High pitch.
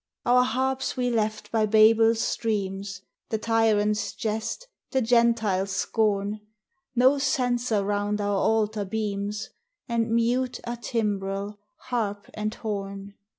Yes: high, 220 Hz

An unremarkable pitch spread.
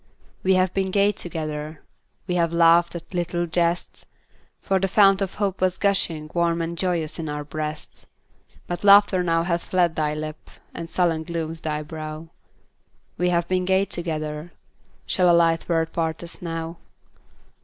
No: narrow, 2.2 semitones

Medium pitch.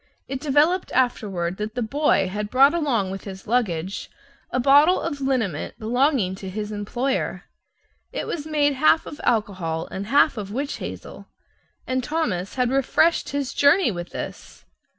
No: high, 245 Hz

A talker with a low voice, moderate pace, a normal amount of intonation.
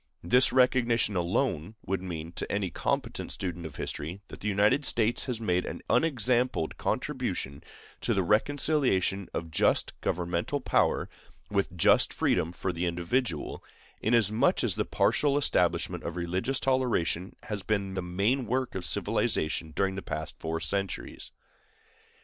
No: low, 100 Hz; average, 145 wpm; wide, 5.9 semitones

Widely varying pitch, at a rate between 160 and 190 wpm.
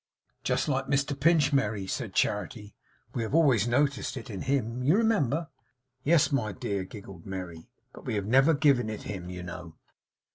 Yes: wide, 5.9 semitones; average, 175 wpm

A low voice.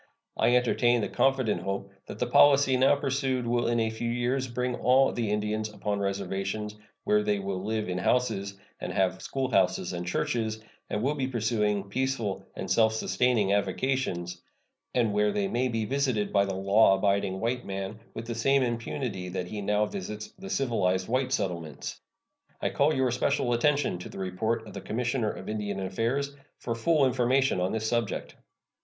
Yes: low, 110 Hz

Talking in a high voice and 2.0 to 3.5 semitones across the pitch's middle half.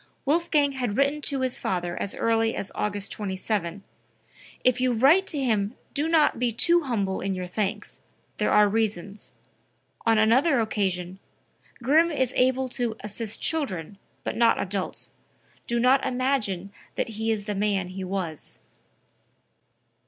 No: high, 225 Hz; average, 4.7 semitones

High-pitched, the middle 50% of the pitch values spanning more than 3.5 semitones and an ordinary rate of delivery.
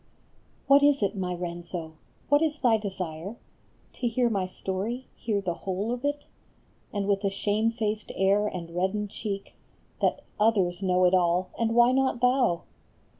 Yes: high, 205 Hz; average, 4.3 semitones; average, 165 wpm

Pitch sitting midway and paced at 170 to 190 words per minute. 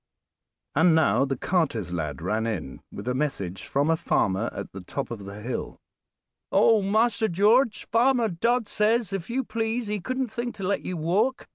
Yes: medium, 180 Hz; average, 180 wpm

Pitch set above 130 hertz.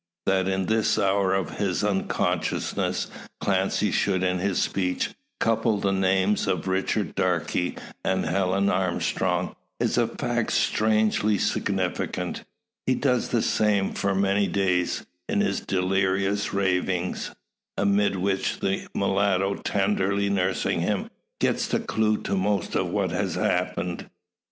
No: very low, 95 Hz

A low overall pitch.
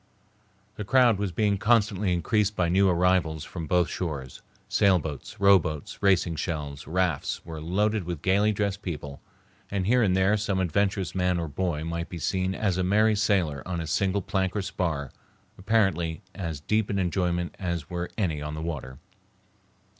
Yes: very low, 90 Hz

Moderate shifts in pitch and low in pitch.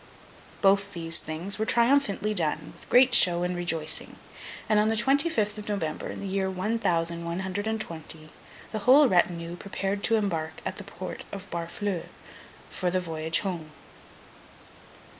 No: average, 4.0 semitones; high, 190 Hz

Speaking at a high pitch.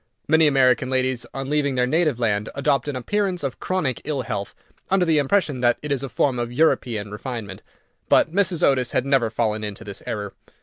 No: low, 130 Hz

